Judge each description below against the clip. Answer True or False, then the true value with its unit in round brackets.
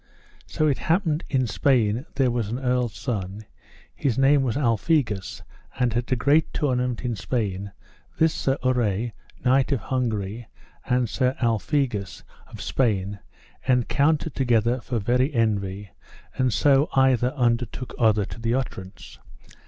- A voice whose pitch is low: True (125 Hz)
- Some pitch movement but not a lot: True (3.4 semitones)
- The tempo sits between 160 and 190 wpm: False (135 wpm)